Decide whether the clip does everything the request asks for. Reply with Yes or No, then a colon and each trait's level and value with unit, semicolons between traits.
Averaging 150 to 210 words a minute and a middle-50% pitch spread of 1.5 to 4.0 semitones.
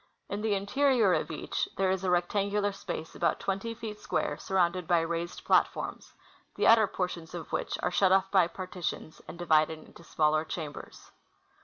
Yes: average, 175 wpm; average, 3.0 semitones